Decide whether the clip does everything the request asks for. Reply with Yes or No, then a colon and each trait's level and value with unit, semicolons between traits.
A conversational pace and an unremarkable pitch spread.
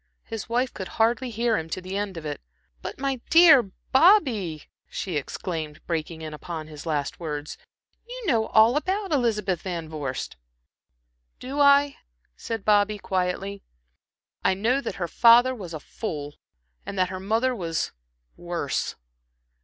No: average, 150 wpm; wide, 6.9 semitones